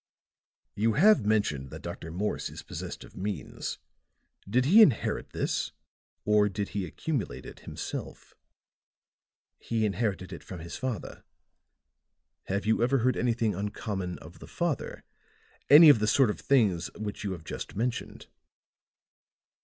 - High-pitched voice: No, low, 105 Hz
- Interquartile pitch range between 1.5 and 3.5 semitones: No, average, 4.5 semitones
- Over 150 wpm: No, average, 140 wpm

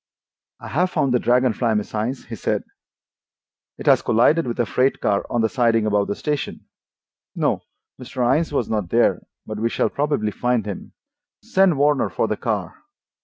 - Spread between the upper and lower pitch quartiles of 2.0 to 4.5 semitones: Yes, average, 4.2 semitones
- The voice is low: Yes, low, 120 Hz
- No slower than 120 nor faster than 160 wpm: No, average, 180 wpm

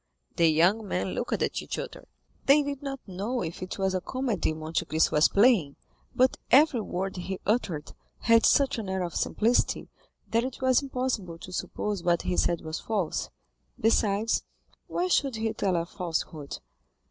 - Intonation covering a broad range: Yes, wide, 6.2 semitones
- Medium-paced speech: Yes, average, 170 wpm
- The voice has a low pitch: No, high, 200 Hz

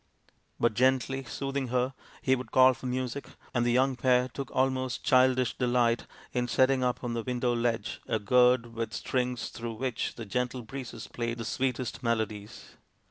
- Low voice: Yes, low, 125 Hz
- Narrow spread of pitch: Yes, narrow, 1.6 semitones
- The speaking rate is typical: Yes, average, 170 wpm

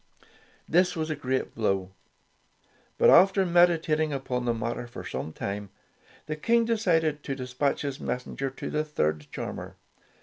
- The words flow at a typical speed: Yes, average, 155 wpm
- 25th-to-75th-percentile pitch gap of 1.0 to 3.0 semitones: No, average, 5.2 semitones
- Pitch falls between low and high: Yes, medium, 145 Hz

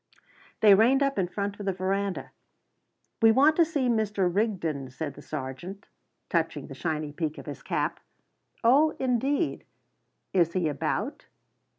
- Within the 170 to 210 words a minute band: No, average, 150 wpm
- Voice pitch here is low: No, high, 200 Hz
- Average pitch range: No, wide, 6.7 semitones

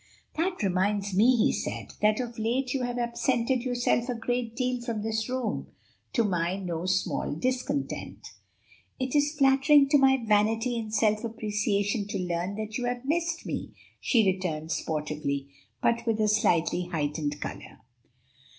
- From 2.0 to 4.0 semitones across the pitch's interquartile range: No, average, 4.6 semitones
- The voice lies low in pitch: No, high, 225 Hz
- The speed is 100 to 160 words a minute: Yes, average, 155 wpm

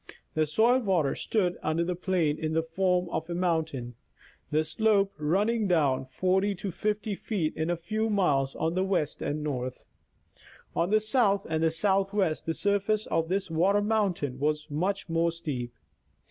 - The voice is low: No, medium, 175 Hz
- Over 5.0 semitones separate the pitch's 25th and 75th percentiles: No, average, 4.2 semitones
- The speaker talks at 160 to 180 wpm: Yes, average, 170 wpm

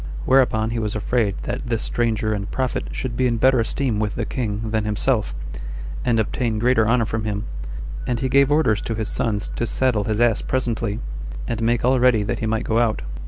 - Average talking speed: No, fast, 210 wpm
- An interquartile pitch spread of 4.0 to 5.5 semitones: No, narrow, 2.4 semitones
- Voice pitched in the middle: No, low, 115 Hz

